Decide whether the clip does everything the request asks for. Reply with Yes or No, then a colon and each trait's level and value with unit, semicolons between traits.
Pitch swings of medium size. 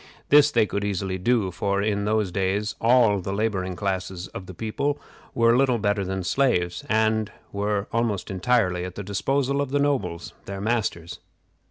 Yes: average, 3.6 semitones